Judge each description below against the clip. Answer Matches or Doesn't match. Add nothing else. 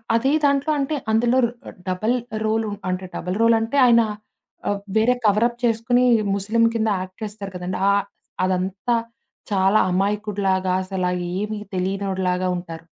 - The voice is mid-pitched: Doesn't match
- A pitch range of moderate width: Matches